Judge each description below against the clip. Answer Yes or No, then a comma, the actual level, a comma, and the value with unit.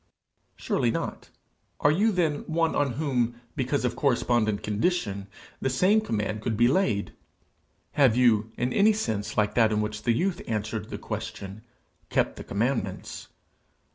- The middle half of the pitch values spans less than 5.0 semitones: No, wide, 5.5 semitones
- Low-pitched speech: Yes, low, 120 Hz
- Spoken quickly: No, average, 150 wpm